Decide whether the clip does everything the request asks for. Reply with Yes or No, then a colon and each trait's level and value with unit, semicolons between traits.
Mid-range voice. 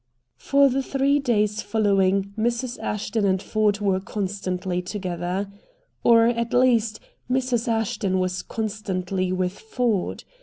No: high, 210 Hz